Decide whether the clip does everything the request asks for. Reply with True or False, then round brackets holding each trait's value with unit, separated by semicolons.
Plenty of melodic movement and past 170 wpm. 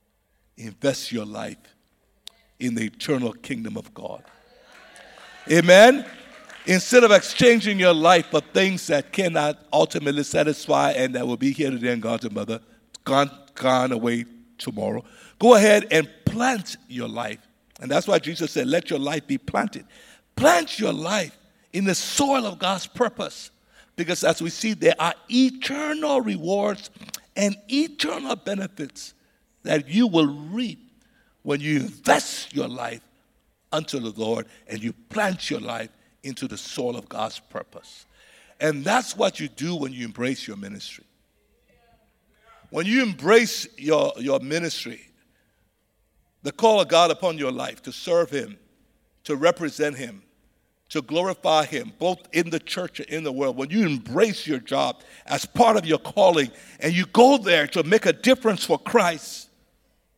False (7.5 semitones; 155 wpm)